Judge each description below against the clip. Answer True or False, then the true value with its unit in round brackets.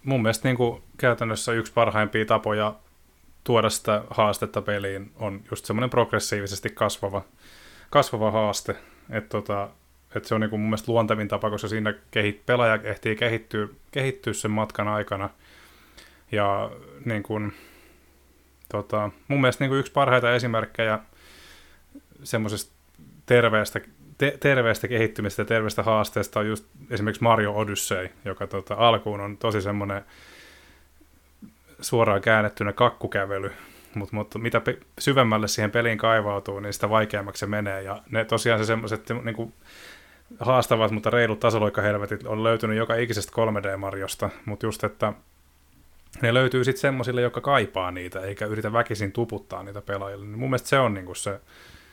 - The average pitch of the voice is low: True (110 Hz)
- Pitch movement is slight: True (2.3 semitones)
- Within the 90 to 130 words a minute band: False (140 wpm)